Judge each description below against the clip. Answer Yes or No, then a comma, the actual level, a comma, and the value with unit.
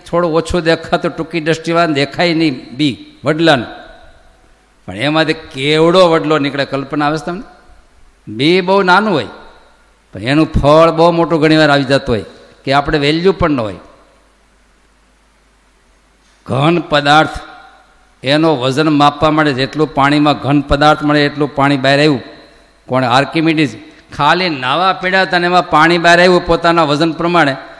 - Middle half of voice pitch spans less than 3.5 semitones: Yes, average, 2.8 semitones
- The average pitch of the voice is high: No, medium, 155 Hz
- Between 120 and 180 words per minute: Yes, fast, 140 wpm